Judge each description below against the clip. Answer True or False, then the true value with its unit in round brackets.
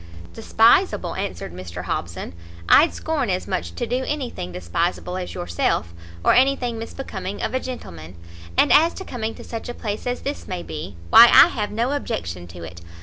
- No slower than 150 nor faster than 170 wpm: False (185 wpm)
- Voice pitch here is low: False (195 Hz)